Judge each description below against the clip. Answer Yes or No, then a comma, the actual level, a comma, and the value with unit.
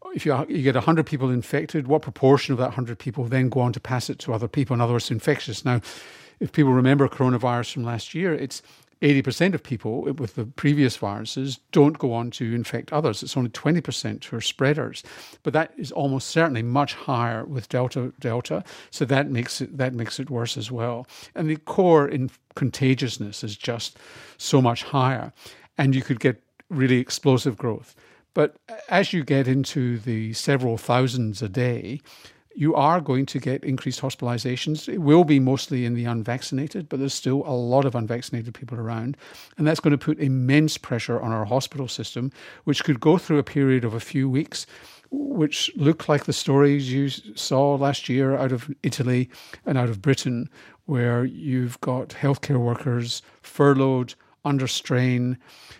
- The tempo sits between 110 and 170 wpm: No, average, 185 wpm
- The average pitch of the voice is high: No, low, 130 Hz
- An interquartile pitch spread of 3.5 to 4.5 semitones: No, average, 2.8 semitones